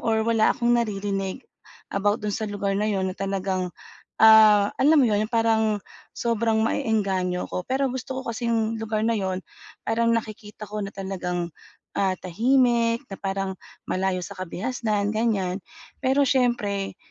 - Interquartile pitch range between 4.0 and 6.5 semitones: No, average, 2.9 semitones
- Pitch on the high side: Yes, high, 215 Hz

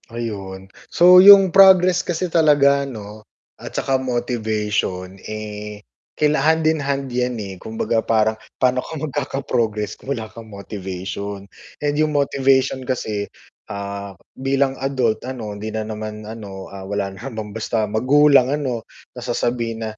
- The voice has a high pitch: No, low, 115 Hz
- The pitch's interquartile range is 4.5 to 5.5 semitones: Yes, average, 4.8 semitones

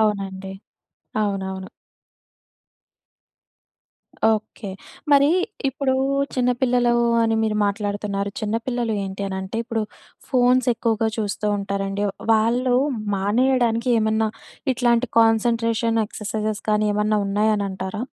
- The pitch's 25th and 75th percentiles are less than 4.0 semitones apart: Yes, average, 2.8 semitones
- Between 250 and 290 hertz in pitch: No, high, 220 Hz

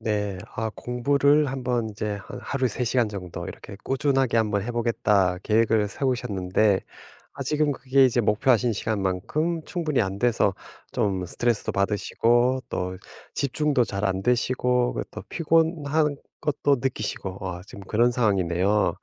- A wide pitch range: No, average, 4.7 semitones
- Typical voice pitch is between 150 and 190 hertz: No, low, 115 Hz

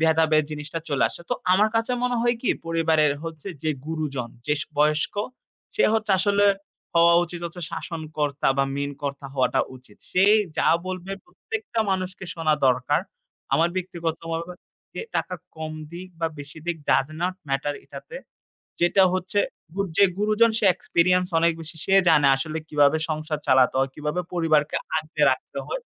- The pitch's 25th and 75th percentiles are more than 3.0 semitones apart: Yes, average, 3.5 semitones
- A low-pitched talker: No, medium, 165 Hz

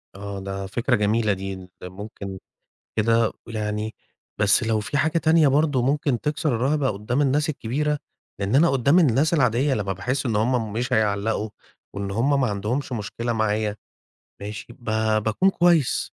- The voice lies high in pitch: No, low, 115 Hz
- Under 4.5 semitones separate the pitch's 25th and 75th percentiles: No, average, 5.1 semitones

